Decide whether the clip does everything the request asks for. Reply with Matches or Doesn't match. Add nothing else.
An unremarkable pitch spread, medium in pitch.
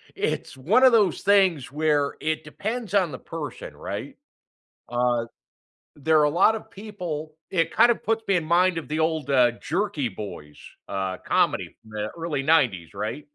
Doesn't match